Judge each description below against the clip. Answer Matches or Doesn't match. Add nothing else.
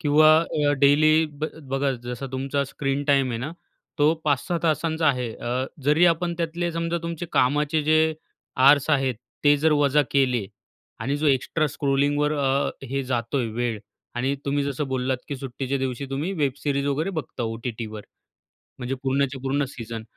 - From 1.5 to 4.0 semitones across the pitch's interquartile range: Matches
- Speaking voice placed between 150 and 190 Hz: Doesn't match